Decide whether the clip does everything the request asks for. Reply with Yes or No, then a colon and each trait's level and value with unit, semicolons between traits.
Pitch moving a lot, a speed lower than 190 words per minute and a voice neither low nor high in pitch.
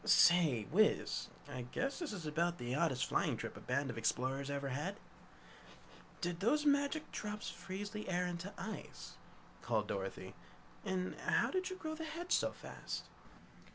Yes: wide, 8.6 semitones; average, 155 wpm; medium, 180 Hz